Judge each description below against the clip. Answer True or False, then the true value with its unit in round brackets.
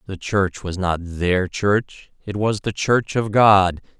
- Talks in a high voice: False (100 Hz)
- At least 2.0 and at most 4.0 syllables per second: True (3.4 syllables/s)